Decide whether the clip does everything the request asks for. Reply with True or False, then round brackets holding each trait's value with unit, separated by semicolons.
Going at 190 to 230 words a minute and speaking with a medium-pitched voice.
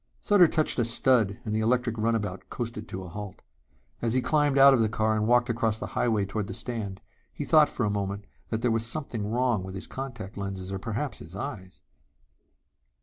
False (205 wpm; 110 Hz)